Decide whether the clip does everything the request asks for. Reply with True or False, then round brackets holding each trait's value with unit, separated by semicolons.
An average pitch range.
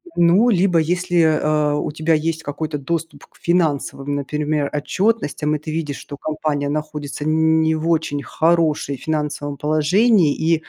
False (1.9 semitones)